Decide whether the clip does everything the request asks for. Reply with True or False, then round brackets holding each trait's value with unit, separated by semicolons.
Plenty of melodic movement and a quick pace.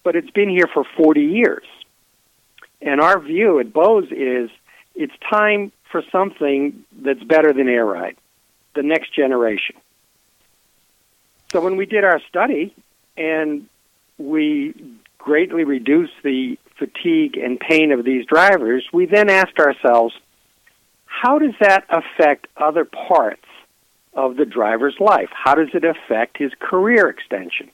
False (7.0 semitones; 135 wpm)